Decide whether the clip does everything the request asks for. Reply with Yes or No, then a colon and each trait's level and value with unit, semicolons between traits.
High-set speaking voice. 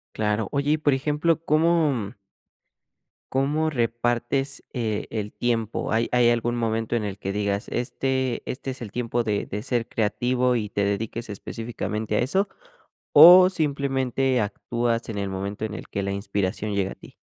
No: low, 120 Hz